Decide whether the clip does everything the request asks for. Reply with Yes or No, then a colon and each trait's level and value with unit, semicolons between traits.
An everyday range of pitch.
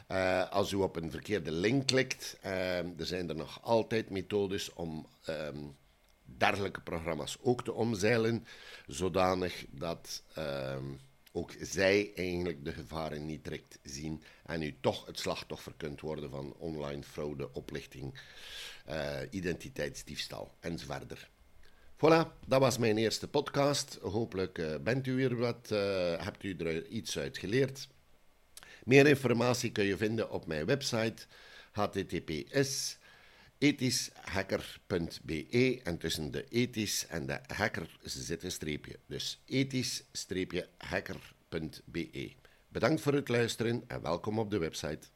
No: wide, 7.1 semitones